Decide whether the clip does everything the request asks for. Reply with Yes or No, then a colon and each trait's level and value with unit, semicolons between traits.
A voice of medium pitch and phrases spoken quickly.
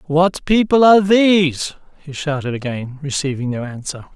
No: medium, 155 Hz; average, 145 wpm